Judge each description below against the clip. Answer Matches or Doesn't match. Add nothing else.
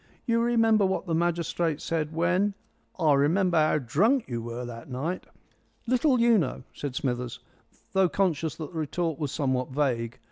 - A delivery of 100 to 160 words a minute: Doesn't match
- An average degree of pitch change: Doesn't match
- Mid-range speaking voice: Matches